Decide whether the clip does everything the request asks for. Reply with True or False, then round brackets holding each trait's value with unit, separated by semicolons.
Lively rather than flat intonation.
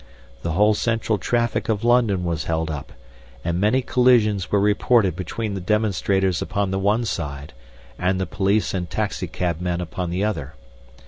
False (3.5 semitones)